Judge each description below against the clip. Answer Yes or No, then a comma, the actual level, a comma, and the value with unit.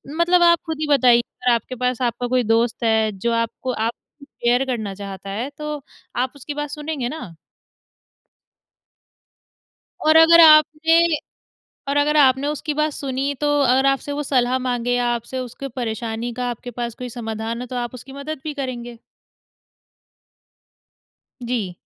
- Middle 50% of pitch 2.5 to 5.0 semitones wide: Yes, average, 3.6 semitones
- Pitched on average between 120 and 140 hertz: No, very high, 250 Hz